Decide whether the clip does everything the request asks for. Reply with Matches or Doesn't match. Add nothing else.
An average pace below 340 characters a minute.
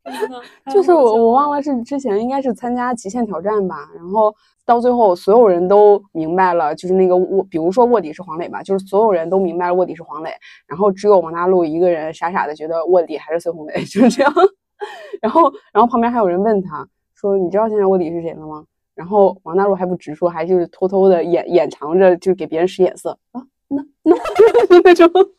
Matches